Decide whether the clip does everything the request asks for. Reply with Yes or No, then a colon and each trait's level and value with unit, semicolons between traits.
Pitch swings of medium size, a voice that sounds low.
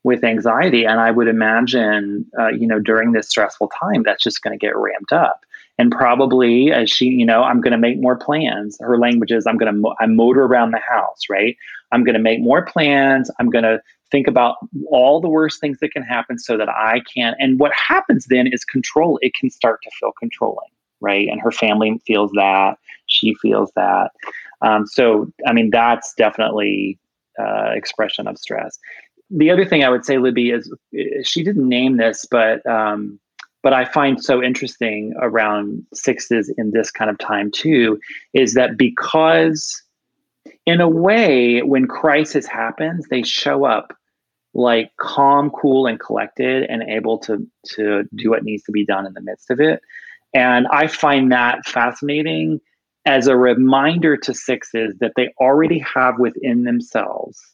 Yes: average, 4.0 semitones; low, 120 Hz